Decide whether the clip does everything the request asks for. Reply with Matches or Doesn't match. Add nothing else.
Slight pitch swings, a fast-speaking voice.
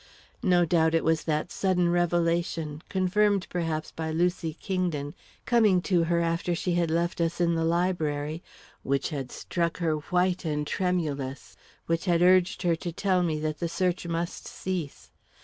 Doesn't match